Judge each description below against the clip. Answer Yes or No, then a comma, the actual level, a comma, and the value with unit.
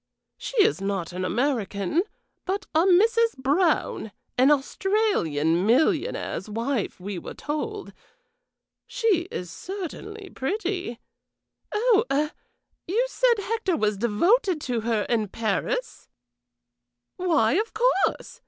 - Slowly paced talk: Yes, slow, 110 wpm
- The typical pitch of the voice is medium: No, very high, 315 Hz